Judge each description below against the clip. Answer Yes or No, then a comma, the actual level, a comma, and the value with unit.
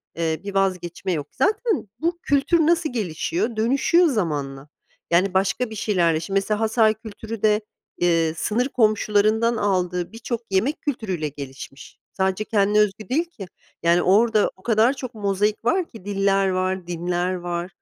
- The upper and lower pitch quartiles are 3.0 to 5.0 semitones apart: Yes, average, 4.4 semitones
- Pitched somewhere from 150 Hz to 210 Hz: Yes, high, 205 Hz